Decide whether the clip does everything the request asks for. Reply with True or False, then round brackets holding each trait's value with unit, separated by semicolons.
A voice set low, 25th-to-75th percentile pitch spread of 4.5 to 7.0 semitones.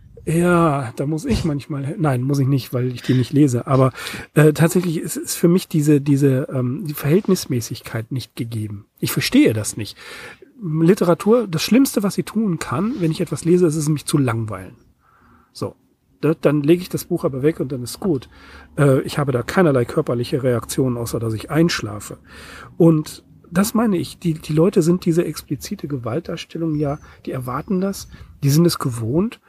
False (155 Hz; 4.9 semitones)